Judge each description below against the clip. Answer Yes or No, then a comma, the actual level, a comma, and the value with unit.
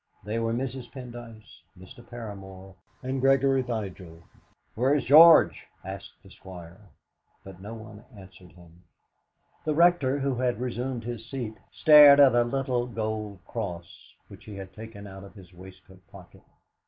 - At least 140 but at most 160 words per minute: Yes, average, 145 wpm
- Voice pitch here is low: Yes, low, 110 Hz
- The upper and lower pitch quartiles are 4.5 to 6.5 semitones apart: Yes, average, 5.0 semitones